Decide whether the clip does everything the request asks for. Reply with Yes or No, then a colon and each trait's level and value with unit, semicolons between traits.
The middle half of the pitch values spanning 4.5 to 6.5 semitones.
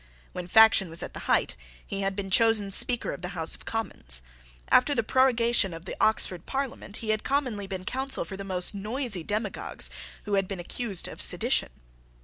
No: average, 3.8 semitones